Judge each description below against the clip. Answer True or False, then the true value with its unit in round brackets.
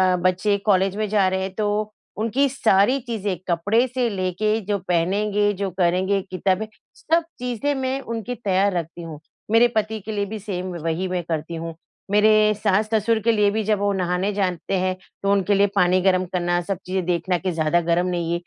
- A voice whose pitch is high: True (195 Hz)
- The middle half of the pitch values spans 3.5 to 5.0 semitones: False (2.9 semitones)